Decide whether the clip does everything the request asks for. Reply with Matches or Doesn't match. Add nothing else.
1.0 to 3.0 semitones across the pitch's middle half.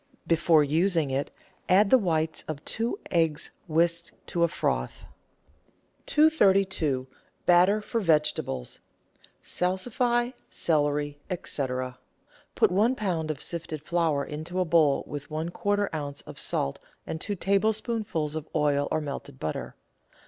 Doesn't match